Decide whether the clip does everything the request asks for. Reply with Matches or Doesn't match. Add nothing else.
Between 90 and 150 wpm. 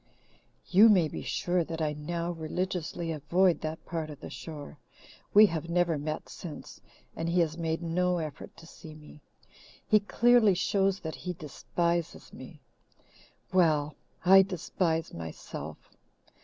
Matches